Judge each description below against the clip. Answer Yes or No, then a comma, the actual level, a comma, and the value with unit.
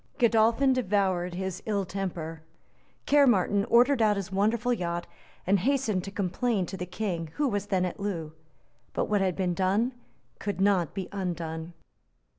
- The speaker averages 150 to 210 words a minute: Yes, average, 155 wpm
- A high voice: Yes, high, 195 Hz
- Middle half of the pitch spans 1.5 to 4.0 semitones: Yes, average, 3.4 semitones